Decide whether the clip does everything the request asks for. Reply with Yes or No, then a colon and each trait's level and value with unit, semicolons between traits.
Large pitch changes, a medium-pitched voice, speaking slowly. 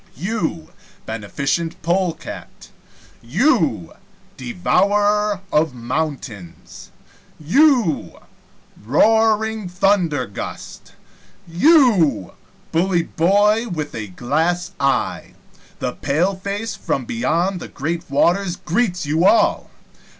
Yes: wide, 6.0 semitones; medium, 175 Hz; slow, 80 wpm